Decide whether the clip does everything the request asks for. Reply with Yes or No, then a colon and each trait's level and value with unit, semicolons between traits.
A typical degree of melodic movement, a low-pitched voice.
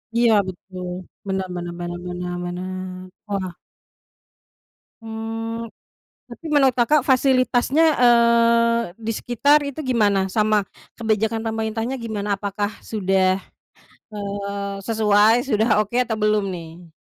No: average, 3.3 semitones; high, 215 Hz